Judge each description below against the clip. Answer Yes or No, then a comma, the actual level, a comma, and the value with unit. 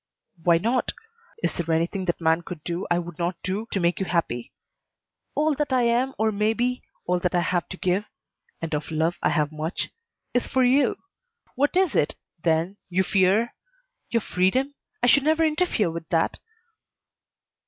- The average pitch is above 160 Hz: Yes, medium, 185 Hz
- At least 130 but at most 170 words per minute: No, average, 180 wpm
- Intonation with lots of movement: Yes, wide, 6.4 semitones